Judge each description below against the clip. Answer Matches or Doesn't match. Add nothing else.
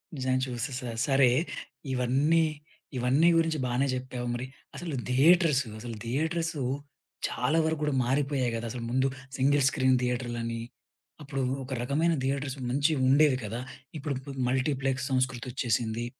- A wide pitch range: Doesn't match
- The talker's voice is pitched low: Matches